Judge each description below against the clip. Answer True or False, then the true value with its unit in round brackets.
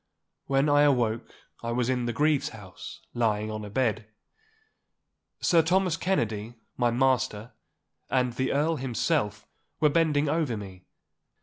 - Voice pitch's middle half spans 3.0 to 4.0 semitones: False (5.1 semitones)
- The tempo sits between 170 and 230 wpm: False (135 wpm)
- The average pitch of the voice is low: True (125 Hz)